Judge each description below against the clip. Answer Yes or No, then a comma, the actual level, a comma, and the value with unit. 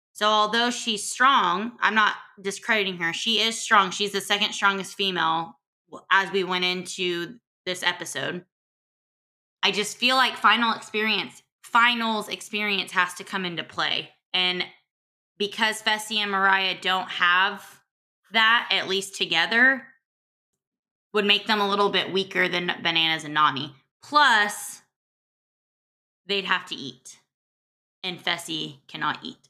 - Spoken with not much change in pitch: No, average, 3.2 semitones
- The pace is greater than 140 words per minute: No, slow, 135 wpm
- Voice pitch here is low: No, high, 195 Hz